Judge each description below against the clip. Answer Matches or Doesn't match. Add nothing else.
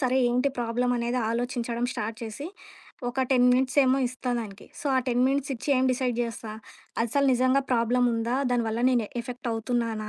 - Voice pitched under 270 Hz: Matches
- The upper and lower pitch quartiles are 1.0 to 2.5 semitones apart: Matches